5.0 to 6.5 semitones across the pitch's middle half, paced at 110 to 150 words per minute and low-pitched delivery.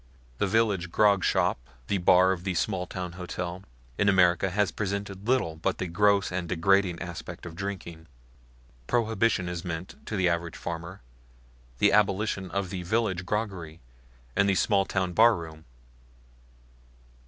No: narrow, 2.6 semitones; average, 140 wpm; very low, 95 Hz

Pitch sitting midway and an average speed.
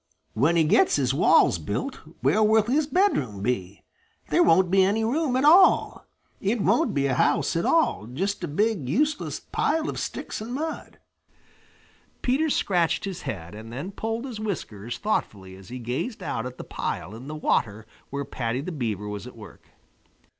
Yes: medium, 165 Hz; average, 180 wpm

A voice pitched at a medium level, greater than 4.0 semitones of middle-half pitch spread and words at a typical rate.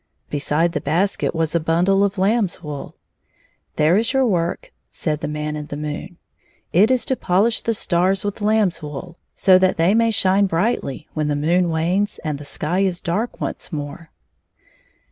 Yes: medium, 175 Hz; average, 4.6 semitones; average, 185 wpm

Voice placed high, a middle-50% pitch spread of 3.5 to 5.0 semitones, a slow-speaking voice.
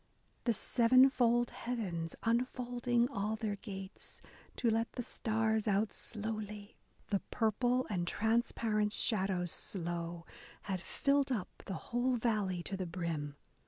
Yes: high, 215 Hz; average, 3.8 semitones; slow, 125 wpm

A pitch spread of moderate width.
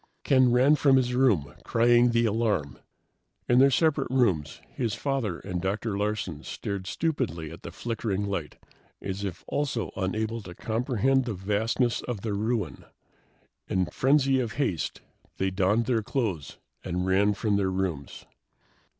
Yes: average, 4.6 semitones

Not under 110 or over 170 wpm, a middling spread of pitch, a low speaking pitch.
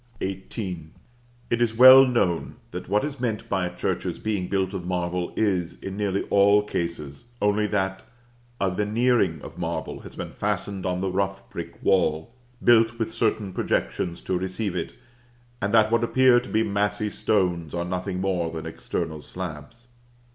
Yes: average, 165 wpm; average, 3.5 semitones; very low, 95 Hz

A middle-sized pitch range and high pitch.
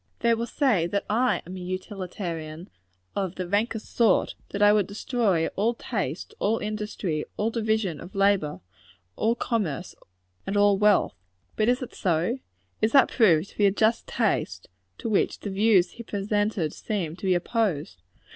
Yes: average, 3.5 semitones; high, 205 Hz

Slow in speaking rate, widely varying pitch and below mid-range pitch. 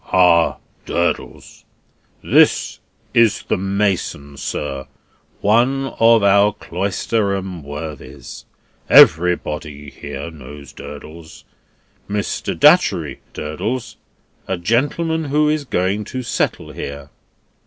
Yes: slow, 90 wpm; wide, 7.1 semitones; very low, 95 Hz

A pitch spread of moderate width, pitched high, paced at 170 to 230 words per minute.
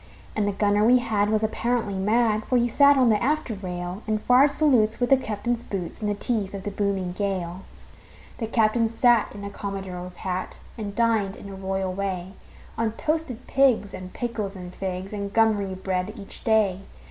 Yes: average, 3.2 semitones; high, 210 Hz; average, 190 wpm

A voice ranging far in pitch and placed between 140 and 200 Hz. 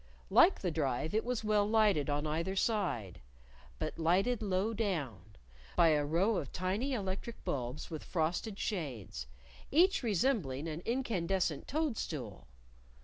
Yes: wide, 6.6 semitones; medium, 185 Hz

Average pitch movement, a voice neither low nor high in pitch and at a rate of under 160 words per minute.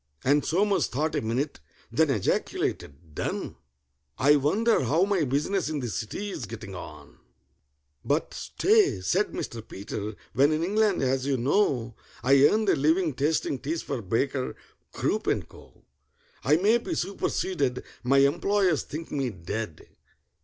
No: wide, 6.1 semitones; medium, 145 Hz; average, 140 wpm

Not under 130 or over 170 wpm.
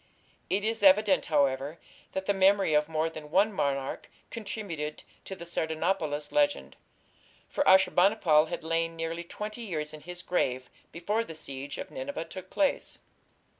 Yes: average, 160 wpm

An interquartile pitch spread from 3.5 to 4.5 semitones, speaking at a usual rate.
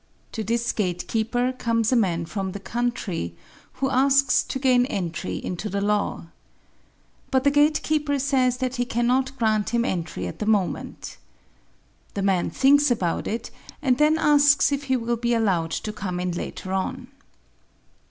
No: average, 5.0 semitones; average, 160 wpm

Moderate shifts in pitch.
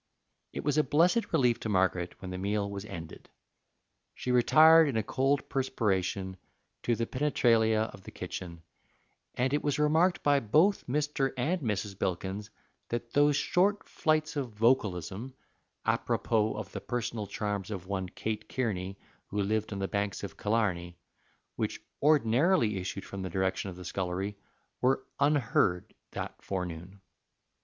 No: wide, 6.2 semitones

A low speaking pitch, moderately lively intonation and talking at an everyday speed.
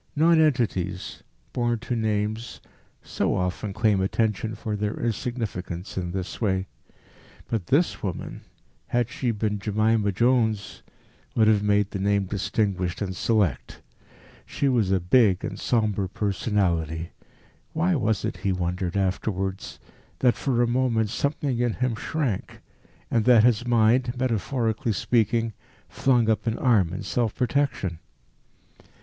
No: low, 110 Hz; average, 3.8 semitones; slow, 130 wpm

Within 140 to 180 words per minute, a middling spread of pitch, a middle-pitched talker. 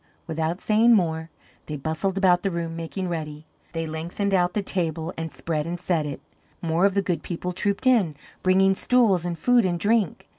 No: average, 190 wpm; average, 3.3 semitones; medium, 175 Hz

